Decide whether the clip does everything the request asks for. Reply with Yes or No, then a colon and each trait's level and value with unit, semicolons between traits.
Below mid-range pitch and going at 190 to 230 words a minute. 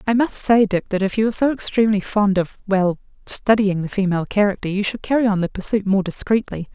No: high, 205 Hz; fast, 205 wpm